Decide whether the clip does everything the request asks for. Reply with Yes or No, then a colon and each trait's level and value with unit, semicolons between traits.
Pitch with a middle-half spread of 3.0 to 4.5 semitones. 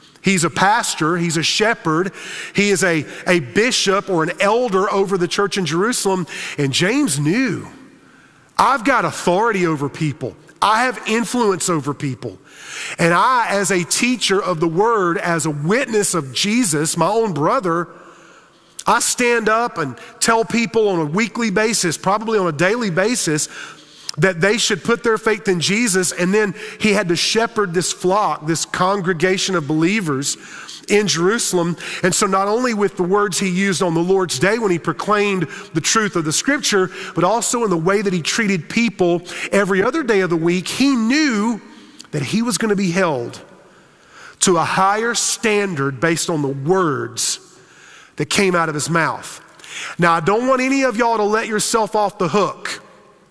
Yes: average, 4.2 semitones